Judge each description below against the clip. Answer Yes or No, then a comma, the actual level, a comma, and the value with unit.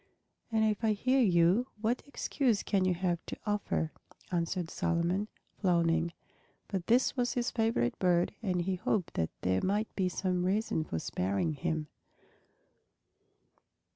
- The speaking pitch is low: No, medium, 185 Hz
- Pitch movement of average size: Yes, average, 4.4 semitones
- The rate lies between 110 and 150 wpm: Yes, average, 140 wpm